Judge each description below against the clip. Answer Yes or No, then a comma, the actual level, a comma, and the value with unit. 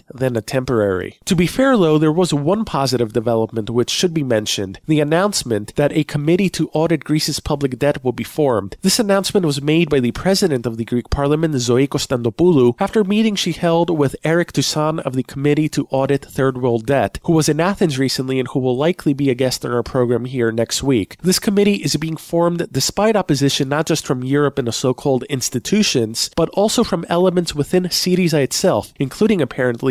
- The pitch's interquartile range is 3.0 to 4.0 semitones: No, average, 5.0 semitones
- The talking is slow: No, average, 200 wpm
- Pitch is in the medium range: Yes, medium, 145 Hz